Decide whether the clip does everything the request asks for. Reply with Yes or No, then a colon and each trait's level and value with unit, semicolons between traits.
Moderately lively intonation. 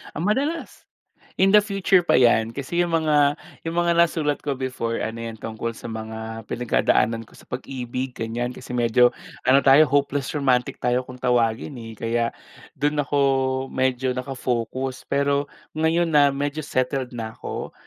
Yes: average, 3.9 semitones